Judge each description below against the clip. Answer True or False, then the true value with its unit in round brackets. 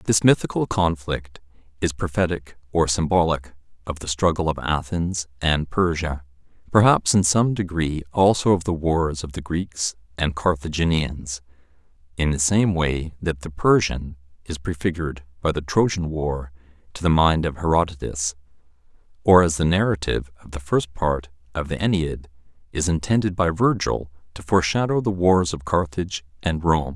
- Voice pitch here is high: False (80 Hz)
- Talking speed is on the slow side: False (150 wpm)